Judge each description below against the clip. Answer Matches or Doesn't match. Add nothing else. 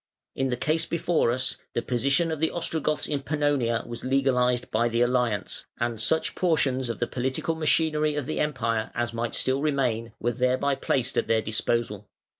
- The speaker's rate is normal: Matches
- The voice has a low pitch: Matches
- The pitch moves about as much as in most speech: Matches